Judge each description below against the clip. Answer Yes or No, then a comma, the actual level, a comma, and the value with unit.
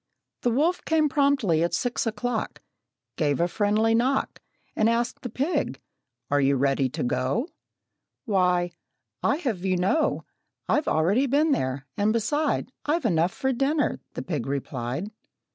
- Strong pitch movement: Yes, wide, 9.0 semitones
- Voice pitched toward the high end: Yes, high, 215 Hz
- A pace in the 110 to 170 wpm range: Yes, average, 145 wpm